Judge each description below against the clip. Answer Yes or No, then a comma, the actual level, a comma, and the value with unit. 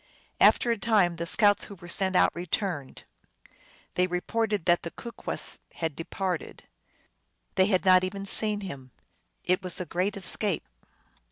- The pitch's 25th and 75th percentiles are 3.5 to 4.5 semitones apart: No, average, 2.8 semitones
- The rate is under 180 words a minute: Yes, average, 150 wpm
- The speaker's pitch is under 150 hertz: No, medium, 185 Hz